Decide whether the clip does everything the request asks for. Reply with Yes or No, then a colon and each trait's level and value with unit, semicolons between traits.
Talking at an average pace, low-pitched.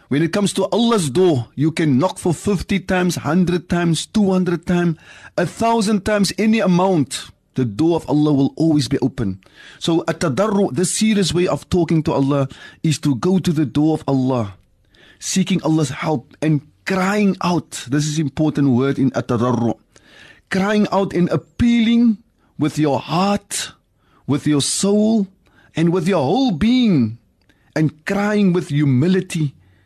No: average, 155 wpm; medium, 165 Hz